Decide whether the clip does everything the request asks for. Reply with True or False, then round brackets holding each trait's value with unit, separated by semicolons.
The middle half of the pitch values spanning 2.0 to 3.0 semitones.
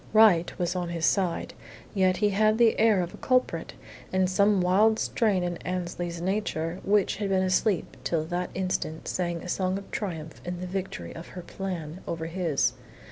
True (2.5 semitones)